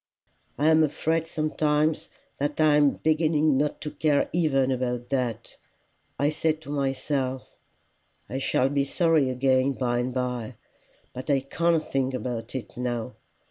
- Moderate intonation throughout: Yes, average, 3.2 semitones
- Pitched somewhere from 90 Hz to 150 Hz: Yes, medium, 140 Hz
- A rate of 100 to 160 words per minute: Yes, average, 145 wpm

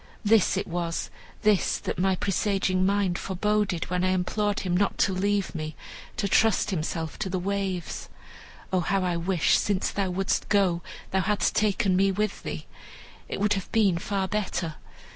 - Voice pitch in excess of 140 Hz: Yes, high, 190 Hz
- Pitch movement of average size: No, narrow, 2.1 semitones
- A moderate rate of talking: Yes, average, 170 wpm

